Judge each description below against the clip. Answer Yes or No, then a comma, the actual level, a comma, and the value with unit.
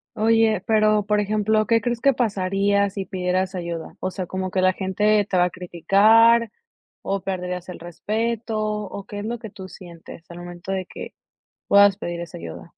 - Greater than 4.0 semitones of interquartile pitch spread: No, average, 2.8 semitones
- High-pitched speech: Yes, high, 195 Hz